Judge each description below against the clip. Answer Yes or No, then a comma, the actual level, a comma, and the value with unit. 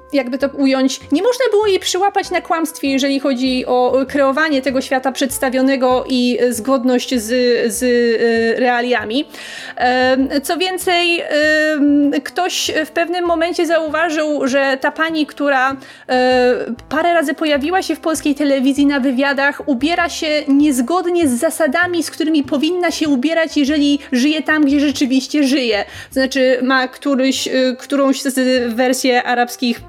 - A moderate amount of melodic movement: Yes, average, 3.4 semitones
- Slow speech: No, average, 130 wpm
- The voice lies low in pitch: No, very high, 280 Hz